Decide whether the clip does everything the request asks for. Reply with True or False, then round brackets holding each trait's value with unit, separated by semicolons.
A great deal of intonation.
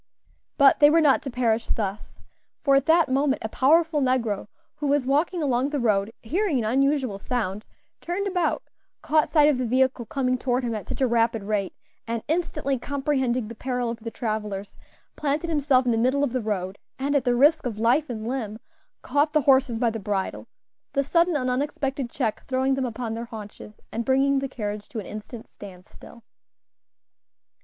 False (4.0 semitones)